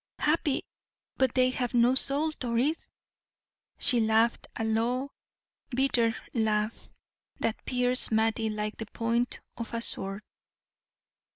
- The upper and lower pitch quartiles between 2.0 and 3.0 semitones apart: Yes, narrow, 2.6 semitones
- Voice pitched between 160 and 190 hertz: No, high, 235 Hz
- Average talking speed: No, slow, 115 wpm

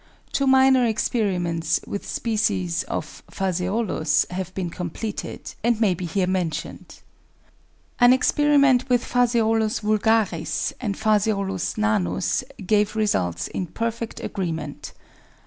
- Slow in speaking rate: Yes, slow, 110 wpm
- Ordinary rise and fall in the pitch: Yes, average, 4.3 semitones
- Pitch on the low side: No, high, 210 Hz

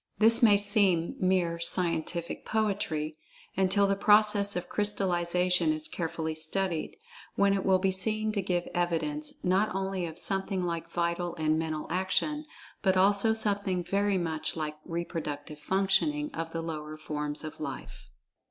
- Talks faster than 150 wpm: No, average, 145 wpm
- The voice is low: No, medium, 180 Hz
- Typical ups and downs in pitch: Yes, average, 3.5 semitones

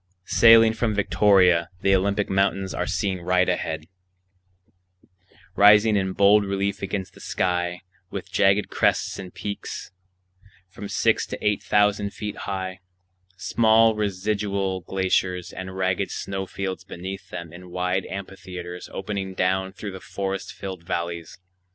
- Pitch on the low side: Yes, very low, 95 Hz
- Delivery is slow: Yes, slow, 130 wpm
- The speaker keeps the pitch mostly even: Yes, narrow, 1.8 semitones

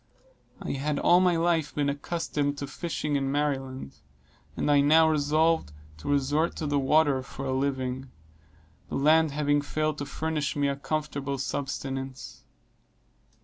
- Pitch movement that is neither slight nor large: No, narrow, 2.1 semitones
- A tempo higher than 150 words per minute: No, average, 145 wpm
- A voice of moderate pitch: Yes, medium, 145 Hz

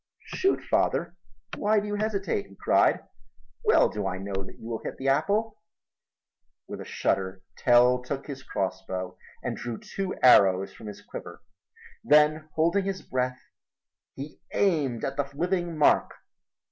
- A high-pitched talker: No, low, 135 Hz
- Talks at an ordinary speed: Yes, average, 150 wpm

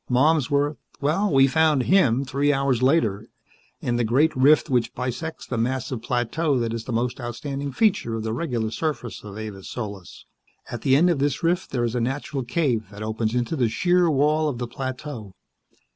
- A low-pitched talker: Yes, low, 130 Hz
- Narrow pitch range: No, average, 4.1 semitones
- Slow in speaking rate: No, average, 190 wpm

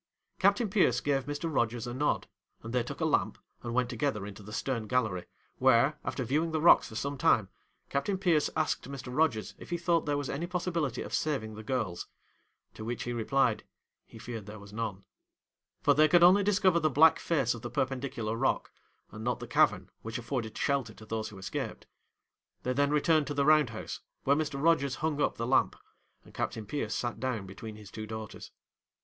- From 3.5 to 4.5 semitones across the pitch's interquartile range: No, wide, 5.4 semitones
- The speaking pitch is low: Yes, low, 130 Hz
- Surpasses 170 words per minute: Yes, fast, 205 wpm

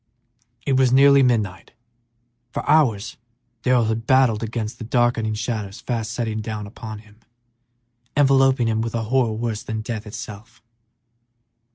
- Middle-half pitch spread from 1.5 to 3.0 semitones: Yes, narrow, 2.5 semitones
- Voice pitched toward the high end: No, low, 115 Hz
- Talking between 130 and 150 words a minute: Yes, average, 140 wpm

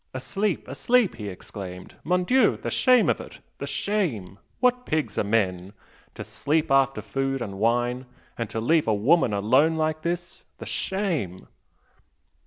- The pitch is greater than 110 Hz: Yes, low, 135 Hz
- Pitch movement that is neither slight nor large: No, wide, 8.6 semitones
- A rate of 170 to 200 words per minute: No, average, 155 wpm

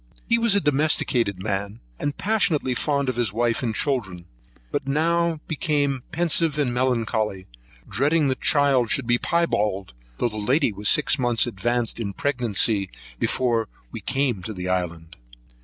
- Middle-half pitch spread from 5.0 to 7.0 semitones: Yes, wide, 5.5 semitones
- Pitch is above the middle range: No, low, 125 Hz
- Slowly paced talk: No, average, 155 wpm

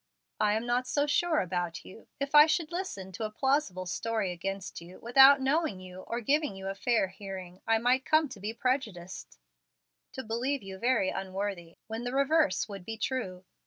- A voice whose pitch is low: No, high, 225 Hz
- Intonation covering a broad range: Yes, wide, 5.9 semitones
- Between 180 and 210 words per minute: Yes, average, 190 wpm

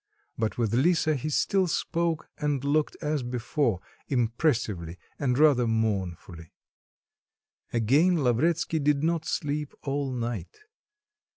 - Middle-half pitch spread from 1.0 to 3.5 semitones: No, average, 5.0 semitones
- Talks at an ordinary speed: No, slow, 110 wpm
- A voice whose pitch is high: No, medium, 140 Hz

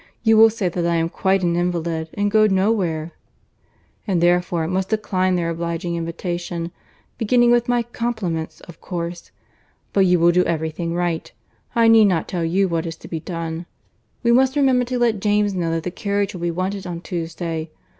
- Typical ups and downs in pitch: Yes, average, 3.6 semitones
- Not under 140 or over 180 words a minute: No, average, 195 wpm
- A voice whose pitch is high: No, medium, 180 Hz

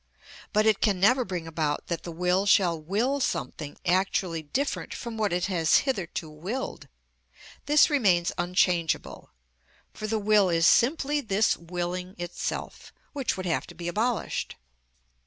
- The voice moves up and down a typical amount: Yes, average, 4.2 semitones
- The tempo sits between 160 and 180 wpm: No, average, 145 wpm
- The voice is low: No, medium, 185 Hz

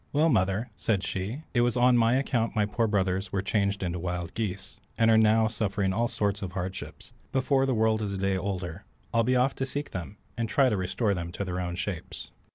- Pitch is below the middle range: Yes, low, 105 Hz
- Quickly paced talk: Yes, fast, 225 wpm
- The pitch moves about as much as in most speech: Yes, average, 3.7 semitones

